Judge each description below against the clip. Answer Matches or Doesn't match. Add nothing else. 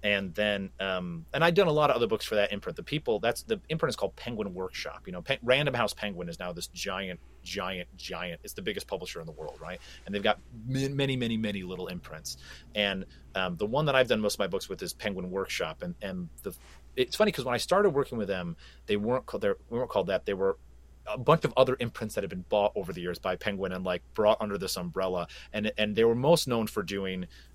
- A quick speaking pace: Matches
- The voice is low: Matches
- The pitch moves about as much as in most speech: Doesn't match